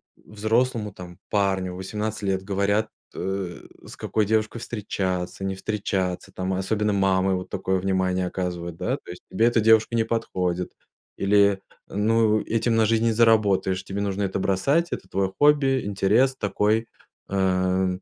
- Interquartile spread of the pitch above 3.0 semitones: No, average, 2.7 semitones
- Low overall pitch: Yes, low, 100 Hz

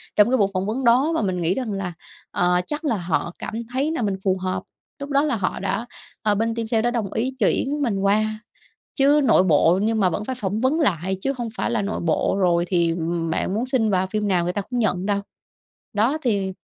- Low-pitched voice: No, high, 210 Hz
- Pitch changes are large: No, average, 4.7 semitones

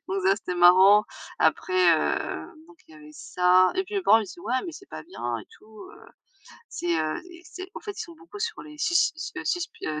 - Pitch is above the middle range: Yes, high, 210 Hz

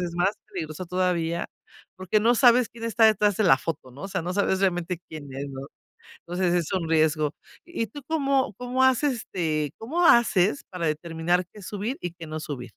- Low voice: No, medium, 185 Hz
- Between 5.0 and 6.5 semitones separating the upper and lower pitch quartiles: Yes, wide, 5.5 semitones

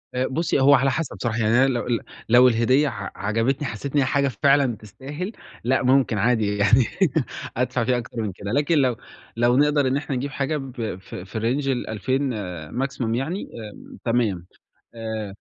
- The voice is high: No, low, 125 Hz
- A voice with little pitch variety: No, average, 3.7 semitones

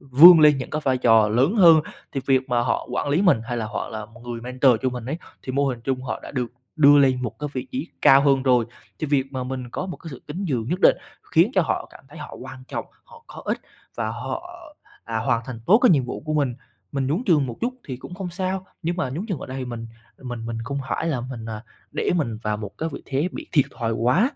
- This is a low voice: Yes, low, 130 Hz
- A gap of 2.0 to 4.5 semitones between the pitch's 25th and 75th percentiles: Yes, average, 4.0 semitones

